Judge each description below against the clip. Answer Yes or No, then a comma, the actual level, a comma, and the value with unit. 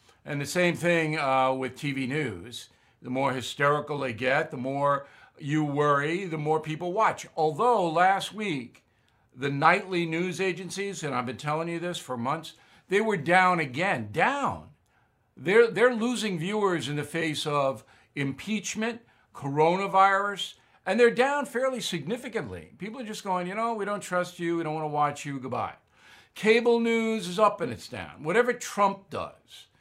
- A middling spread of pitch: No, wide, 6.0 semitones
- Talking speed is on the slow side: No, average, 165 wpm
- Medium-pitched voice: Yes, medium, 170 Hz